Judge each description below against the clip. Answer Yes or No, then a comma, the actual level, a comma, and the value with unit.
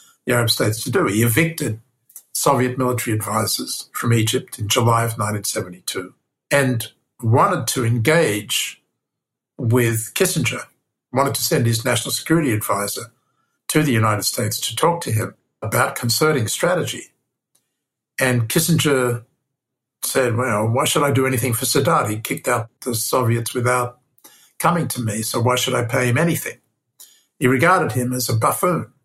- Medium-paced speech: Yes, average, 150 wpm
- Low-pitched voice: Yes, low, 125 Hz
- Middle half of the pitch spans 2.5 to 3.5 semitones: Yes, average, 2.8 semitones